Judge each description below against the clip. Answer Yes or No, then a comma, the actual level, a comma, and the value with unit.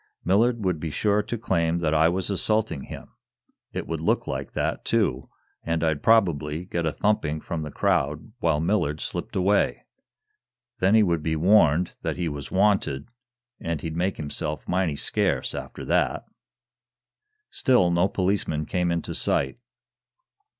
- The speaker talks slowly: No, average, 155 wpm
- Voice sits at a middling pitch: No, very low, 85 Hz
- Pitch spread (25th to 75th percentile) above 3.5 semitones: Yes, average, 4.0 semitones